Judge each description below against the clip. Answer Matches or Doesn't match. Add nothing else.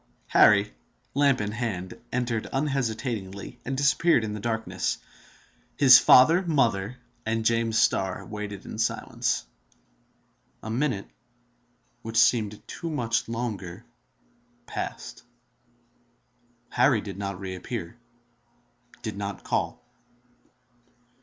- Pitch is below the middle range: Matches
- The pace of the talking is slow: Matches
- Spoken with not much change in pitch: Doesn't match